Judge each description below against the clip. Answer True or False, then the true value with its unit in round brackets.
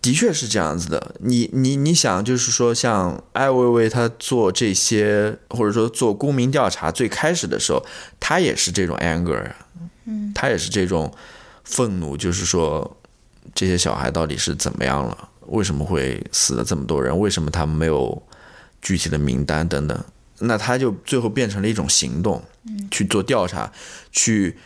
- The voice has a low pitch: True (115 Hz)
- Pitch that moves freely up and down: True (6.0 semitones)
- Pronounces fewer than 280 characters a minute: True (265 characters per minute)